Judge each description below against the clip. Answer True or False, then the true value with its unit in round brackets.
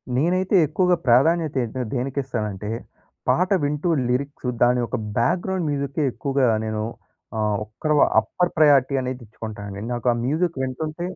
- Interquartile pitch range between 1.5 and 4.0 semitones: False (4.8 semitones)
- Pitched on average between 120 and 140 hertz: True (135 Hz)